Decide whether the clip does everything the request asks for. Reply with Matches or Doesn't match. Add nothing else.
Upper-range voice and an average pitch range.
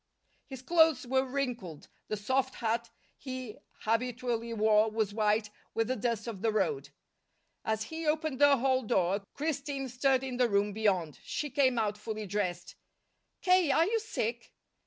Matches